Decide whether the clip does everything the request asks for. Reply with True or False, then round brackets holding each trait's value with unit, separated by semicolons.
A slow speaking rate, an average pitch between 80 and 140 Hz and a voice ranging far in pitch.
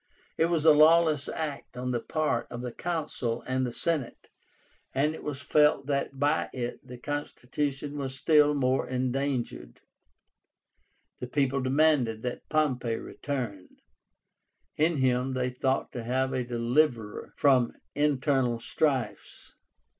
False (130 wpm; 135 Hz; 3.1 semitones)